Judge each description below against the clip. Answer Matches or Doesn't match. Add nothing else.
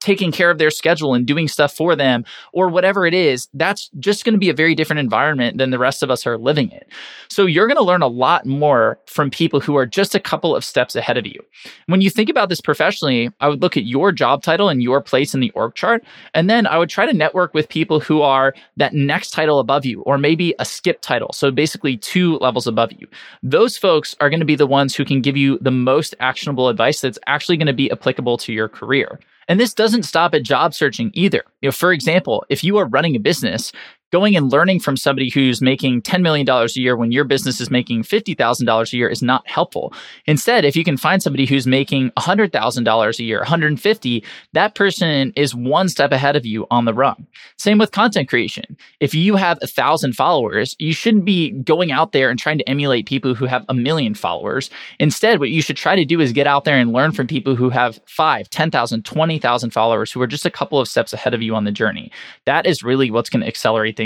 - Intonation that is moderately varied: Matches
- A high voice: Doesn't match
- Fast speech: Matches